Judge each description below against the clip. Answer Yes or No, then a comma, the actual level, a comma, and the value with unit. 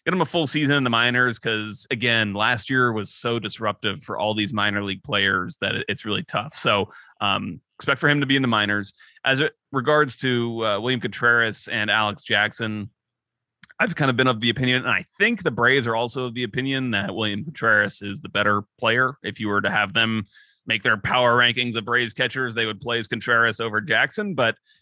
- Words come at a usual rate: No, fast, 215 wpm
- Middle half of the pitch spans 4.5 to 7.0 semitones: No, average, 3.1 semitones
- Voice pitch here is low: Yes, low, 120 Hz